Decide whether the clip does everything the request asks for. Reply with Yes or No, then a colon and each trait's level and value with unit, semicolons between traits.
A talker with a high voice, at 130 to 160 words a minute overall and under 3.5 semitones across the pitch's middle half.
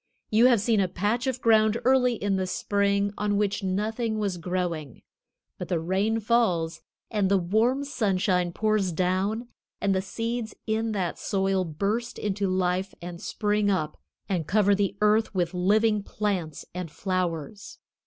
Yes: high, 200 Hz; average, 155 wpm; average, 3.0 semitones